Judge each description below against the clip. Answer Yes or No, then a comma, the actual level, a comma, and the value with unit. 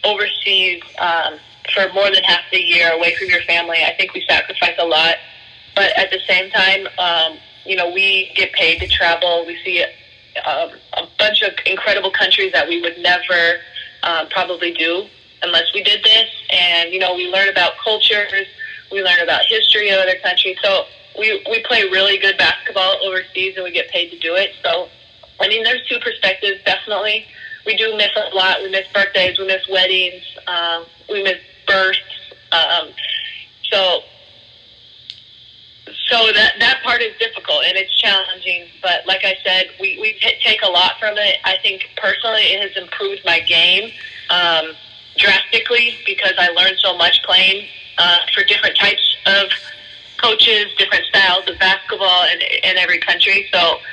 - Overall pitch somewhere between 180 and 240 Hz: Yes, high, 190 Hz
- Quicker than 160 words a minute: Yes, average, 170 wpm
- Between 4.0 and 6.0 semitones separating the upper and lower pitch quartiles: No, average, 3.4 semitones